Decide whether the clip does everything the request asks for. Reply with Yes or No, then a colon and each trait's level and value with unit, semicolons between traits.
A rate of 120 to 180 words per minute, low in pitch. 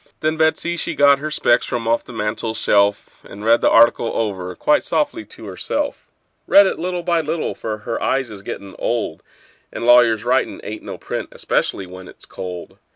No: average, 195 wpm; low, 115 Hz